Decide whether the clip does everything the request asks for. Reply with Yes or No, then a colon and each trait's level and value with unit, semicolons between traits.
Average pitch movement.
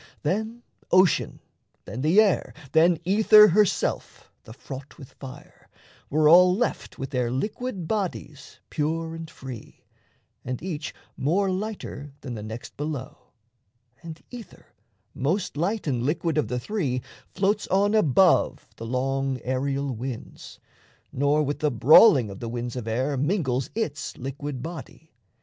No: wide, 6.1 semitones